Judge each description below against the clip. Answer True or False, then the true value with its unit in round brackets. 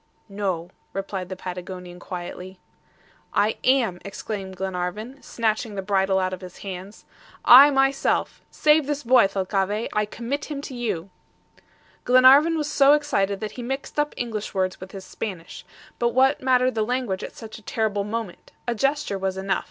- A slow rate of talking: False (165 wpm)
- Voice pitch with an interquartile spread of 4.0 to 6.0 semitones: True (5.2 semitones)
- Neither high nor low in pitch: False (210 Hz)